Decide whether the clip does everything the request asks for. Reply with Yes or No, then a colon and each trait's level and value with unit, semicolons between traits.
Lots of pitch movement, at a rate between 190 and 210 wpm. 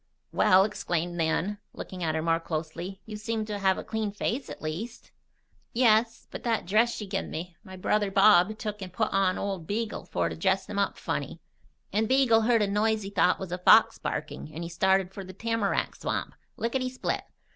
No: average, 3.5 semitones; average, 200 wpm